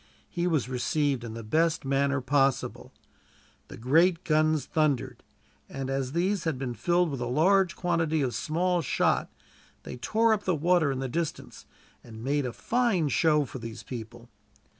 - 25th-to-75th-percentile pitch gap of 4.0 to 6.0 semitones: Yes, average, 4.8 semitones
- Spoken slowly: No, average, 165 wpm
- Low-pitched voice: No, medium, 150 Hz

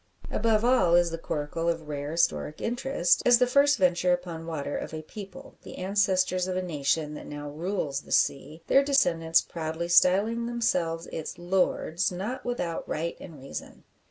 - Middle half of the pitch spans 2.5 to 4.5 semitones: Yes, average, 4.0 semitones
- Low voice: No, medium, 175 Hz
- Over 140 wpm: Yes, average, 170 wpm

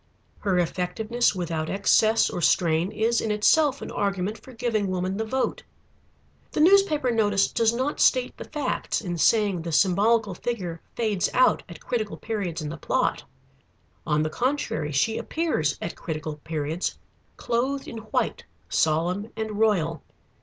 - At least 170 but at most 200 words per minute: No, average, 150 wpm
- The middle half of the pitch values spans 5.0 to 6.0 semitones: Yes, wide, 5.4 semitones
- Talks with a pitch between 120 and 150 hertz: No, high, 205 Hz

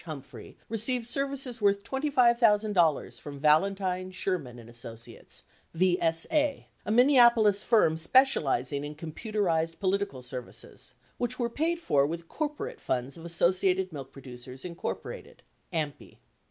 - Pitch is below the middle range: No, medium, 185 Hz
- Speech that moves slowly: Yes, slow, 125 wpm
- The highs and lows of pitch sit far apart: Yes, wide, 7.8 semitones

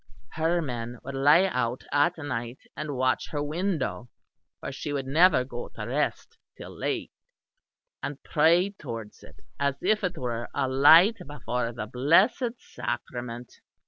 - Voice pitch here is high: No, medium, 140 Hz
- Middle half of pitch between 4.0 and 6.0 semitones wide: Yes, average, 5.1 semitones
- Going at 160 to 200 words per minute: No, average, 145 wpm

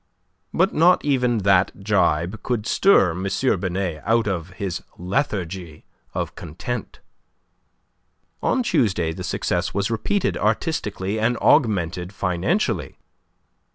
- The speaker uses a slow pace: Yes, slow, 110 wpm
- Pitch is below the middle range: Yes, low, 100 Hz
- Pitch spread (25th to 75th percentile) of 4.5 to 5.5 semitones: Yes, average, 5.1 semitones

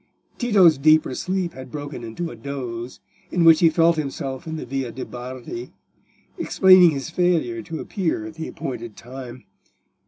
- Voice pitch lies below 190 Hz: Yes, medium, 140 Hz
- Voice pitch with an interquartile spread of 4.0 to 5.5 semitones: Yes, average, 4.9 semitones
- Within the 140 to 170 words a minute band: Yes, average, 160 wpm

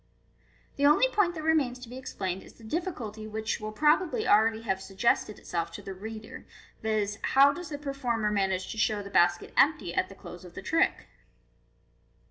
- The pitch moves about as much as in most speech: No, wide, 6.2 semitones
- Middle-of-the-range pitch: No, high, 220 Hz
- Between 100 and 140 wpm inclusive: No, average, 190 wpm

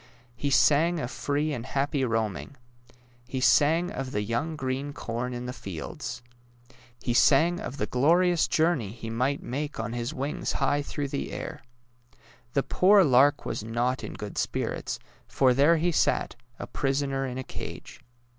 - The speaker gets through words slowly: No, average, 165 wpm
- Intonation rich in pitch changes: No, average, 3.5 semitones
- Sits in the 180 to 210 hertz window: No, low, 135 Hz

